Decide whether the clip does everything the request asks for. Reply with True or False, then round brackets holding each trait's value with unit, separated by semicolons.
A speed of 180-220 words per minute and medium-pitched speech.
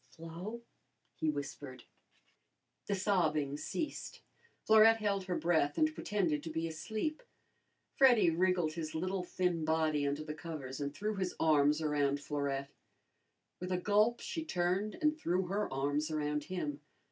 False (145 wpm; 165 Hz)